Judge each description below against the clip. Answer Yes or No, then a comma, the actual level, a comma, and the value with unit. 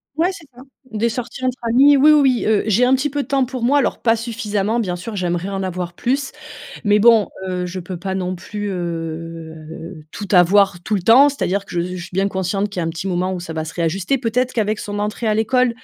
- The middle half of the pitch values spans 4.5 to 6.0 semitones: Yes, average, 5.1 semitones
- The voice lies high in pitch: Yes, high, 205 Hz